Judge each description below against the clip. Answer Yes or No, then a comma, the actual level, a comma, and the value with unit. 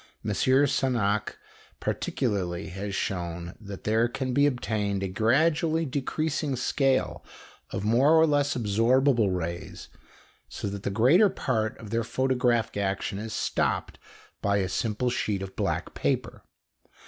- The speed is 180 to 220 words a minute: No, slow, 135 wpm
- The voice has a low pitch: Yes, low, 115 Hz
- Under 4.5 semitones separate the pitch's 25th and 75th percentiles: No, average, 5.0 semitones